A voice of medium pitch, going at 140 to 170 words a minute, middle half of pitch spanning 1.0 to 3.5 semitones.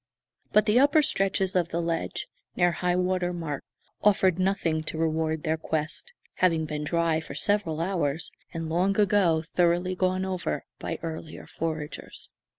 Yes: medium, 170 Hz; average, 155 wpm; average, 2.7 semitones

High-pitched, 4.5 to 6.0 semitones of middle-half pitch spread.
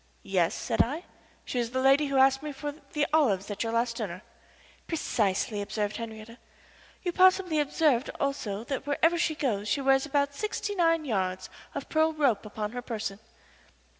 Yes: very high, 265 Hz; wide, 5.6 semitones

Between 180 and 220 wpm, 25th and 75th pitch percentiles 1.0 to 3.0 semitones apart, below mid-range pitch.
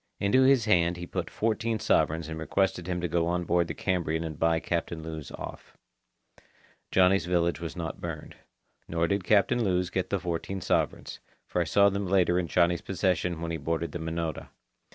Yes: average, 190 wpm; narrow, 2.5 semitones; very low, 85 Hz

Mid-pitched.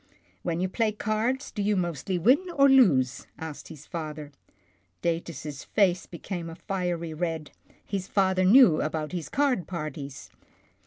Yes: medium, 175 Hz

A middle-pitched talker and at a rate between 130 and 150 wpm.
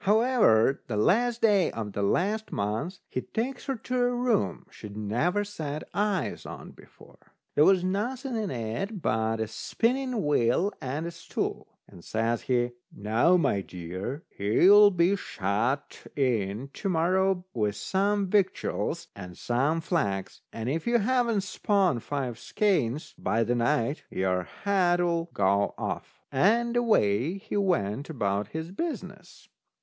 Yes: medium, 165 Hz; average, 145 wpm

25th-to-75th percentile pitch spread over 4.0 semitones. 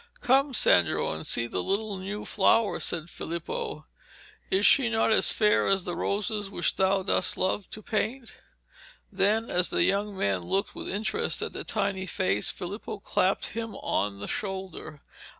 No: average, 3.5 semitones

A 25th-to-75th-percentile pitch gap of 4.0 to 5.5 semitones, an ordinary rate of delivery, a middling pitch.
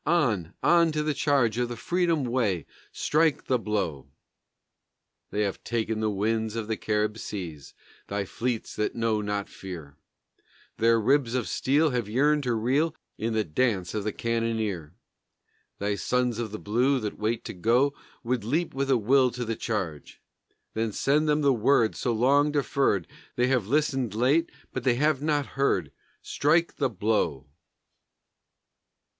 No: average, 4.6 semitones; average, 160 wpm; low, 115 Hz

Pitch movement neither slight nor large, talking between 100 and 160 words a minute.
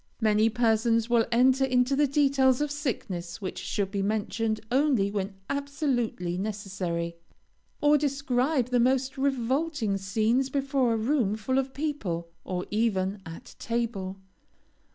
Yes: average, 5.0 semitones; slow, 135 wpm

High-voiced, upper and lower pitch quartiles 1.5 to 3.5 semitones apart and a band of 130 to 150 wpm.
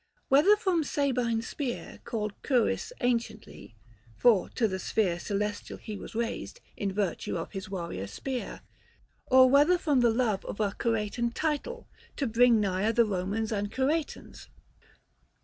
No: high, 230 Hz; average, 4.4 semitones; average, 145 wpm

